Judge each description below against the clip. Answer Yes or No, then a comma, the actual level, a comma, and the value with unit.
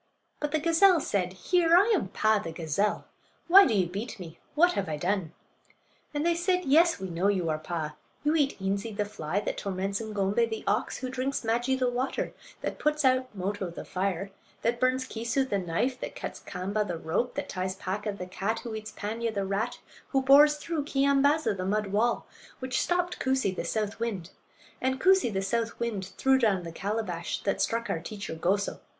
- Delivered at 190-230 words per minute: Yes, average, 200 wpm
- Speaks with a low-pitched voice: No, high, 220 Hz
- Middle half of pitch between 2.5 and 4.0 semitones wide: No, wide, 5.6 semitones